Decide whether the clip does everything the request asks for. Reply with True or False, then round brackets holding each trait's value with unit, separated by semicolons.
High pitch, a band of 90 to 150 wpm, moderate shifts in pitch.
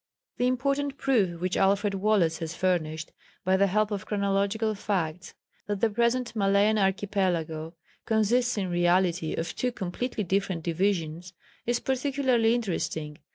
True (200 Hz; 135 wpm; 4.2 semitones)